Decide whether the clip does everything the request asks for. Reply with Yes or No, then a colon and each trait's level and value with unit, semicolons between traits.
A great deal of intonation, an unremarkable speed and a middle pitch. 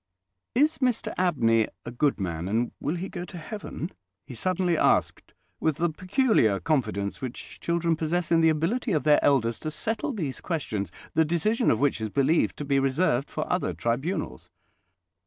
Yes: wide, 6.6 semitones; average, 175 wpm; medium, 155 Hz